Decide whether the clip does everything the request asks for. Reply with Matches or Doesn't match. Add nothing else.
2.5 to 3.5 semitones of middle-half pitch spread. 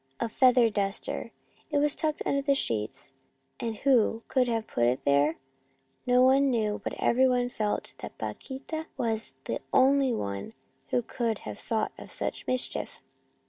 Doesn't match